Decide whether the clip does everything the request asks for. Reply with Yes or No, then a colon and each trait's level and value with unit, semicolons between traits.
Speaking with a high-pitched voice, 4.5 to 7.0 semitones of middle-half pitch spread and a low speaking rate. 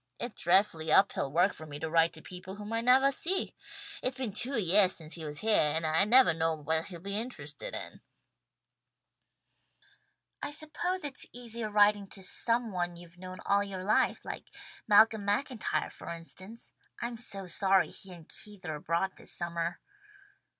No: high, 195 Hz; average, 5.2 semitones; average, 170 wpm